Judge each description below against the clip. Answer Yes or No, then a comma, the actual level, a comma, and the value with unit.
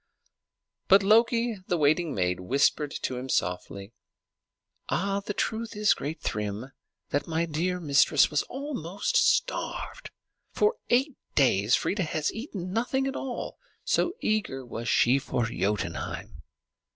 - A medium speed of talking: No, slow, 125 wpm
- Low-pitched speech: No, medium, 170 Hz